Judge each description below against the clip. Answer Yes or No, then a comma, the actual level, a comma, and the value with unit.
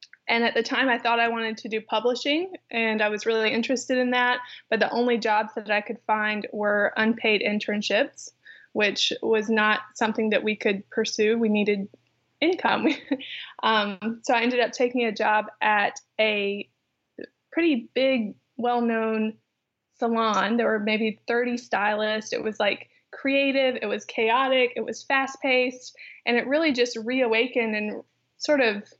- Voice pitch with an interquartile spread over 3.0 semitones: No, narrow, 2.5 semitones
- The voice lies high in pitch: Yes, high, 230 Hz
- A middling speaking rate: Yes, average, 165 wpm